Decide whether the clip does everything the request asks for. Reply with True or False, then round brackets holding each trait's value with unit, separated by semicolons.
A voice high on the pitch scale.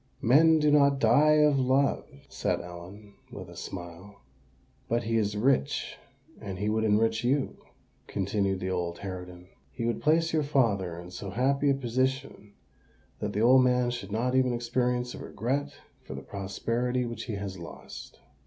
False (115 Hz)